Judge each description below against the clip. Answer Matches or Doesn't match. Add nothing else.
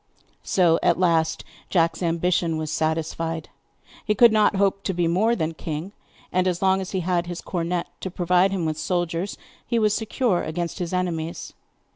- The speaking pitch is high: Doesn't match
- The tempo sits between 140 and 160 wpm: Doesn't match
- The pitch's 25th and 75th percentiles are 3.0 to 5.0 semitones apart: Doesn't match